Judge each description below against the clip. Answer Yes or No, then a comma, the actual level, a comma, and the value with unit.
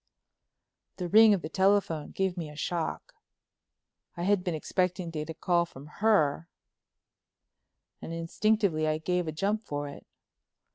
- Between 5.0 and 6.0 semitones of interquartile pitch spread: No, average, 3.8 semitones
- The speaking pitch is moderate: Yes, medium, 175 Hz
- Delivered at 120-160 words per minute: Yes, average, 150 wpm